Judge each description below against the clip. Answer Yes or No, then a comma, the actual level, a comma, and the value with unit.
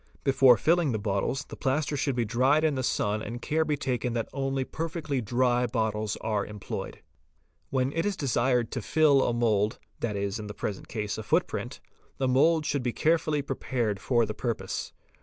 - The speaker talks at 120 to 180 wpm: No, average, 195 wpm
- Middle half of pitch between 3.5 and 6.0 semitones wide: Yes, average, 4.3 semitones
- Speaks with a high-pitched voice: No, low, 125 Hz